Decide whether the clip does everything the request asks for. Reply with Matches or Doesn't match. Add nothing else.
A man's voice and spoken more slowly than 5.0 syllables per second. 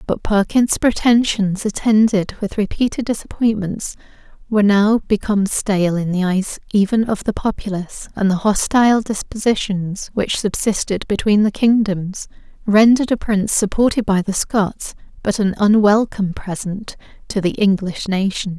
Doesn't match